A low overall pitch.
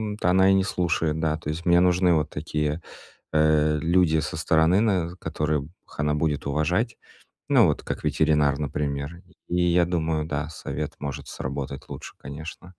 Yes: very low, 80 Hz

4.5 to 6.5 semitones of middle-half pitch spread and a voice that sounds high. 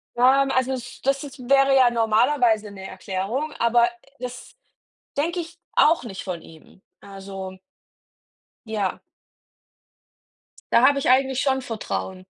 Yes: average, 5.2 semitones; high, 245 Hz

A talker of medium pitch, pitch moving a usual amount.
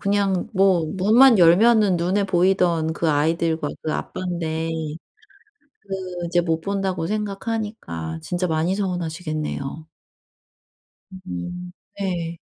Yes: medium, 180 Hz; average, 3.1 semitones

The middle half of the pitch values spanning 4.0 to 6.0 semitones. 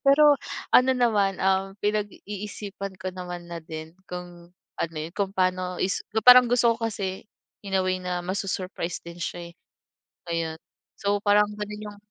No: average, 2.8 semitones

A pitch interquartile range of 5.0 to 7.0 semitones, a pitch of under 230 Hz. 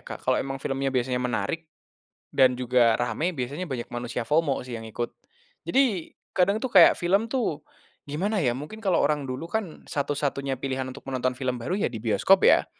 Yes: wide, 5.5 semitones; low, 135 Hz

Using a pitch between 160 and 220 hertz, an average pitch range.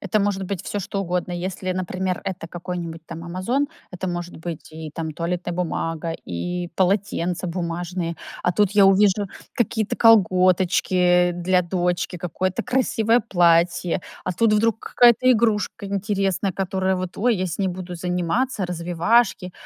No: medium, 185 Hz; narrow, 2.3 semitones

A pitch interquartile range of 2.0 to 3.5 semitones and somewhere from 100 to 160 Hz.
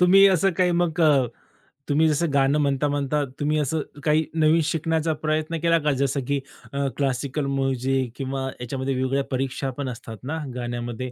Yes: average, 2.9 semitones; medium, 140 Hz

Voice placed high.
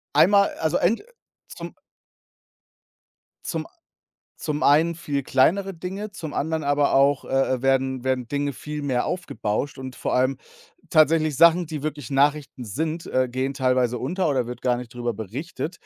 No: medium, 145 Hz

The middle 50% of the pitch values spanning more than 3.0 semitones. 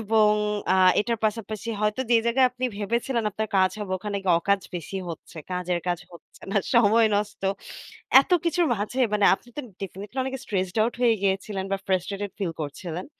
Yes: average, 3.4 semitones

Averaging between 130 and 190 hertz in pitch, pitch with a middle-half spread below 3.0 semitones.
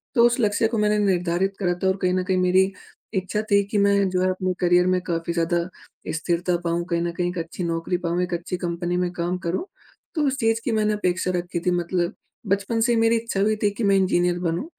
Yes: medium, 185 Hz; narrow, 2.5 semitones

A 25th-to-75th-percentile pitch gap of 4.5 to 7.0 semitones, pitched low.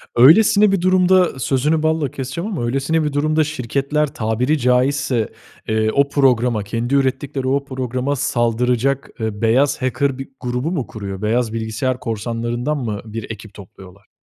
No: average, 3.8 semitones; low, 130 Hz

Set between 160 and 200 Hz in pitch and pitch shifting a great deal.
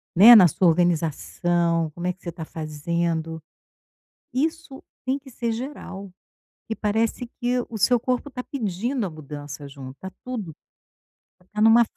Yes: high, 190 Hz; wide, 6.7 semitones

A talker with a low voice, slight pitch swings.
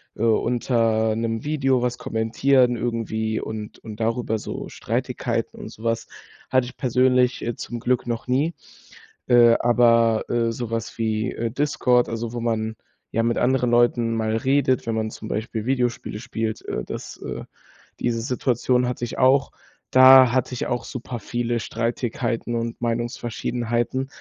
Yes: low, 120 Hz; narrow, 1.8 semitones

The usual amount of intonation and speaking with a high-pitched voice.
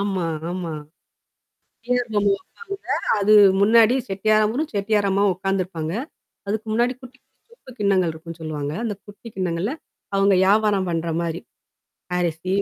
Yes: average, 3.8 semitones; high, 200 Hz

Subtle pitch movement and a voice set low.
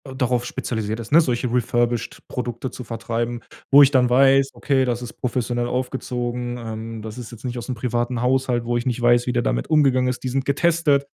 Yes: narrow, 1.7 semitones; low, 125 Hz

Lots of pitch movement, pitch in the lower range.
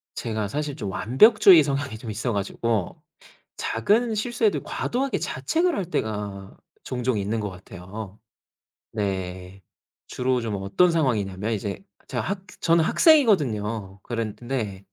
Yes: wide, 8.2 semitones; low, 115 Hz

